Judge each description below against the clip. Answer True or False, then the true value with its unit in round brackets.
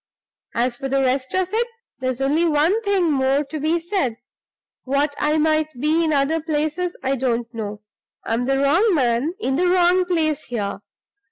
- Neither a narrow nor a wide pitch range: True (4.3 semitones)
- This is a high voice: True (295 Hz)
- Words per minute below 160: False (175 wpm)